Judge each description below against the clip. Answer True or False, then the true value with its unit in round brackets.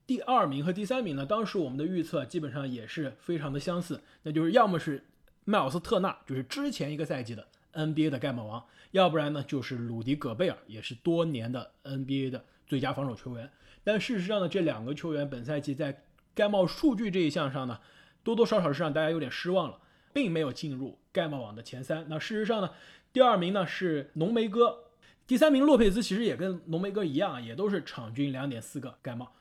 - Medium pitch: True (155 Hz)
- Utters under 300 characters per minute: False (335 characters per minute)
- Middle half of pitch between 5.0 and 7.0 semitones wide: True (5.6 semitones)